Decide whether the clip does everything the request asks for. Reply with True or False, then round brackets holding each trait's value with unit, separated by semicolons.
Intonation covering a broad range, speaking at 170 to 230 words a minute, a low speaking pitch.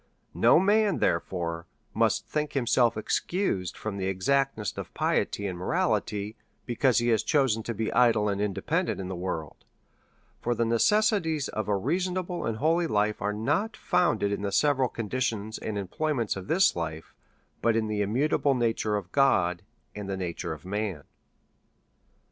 False (5.7 semitones; 160 wpm; 110 Hz)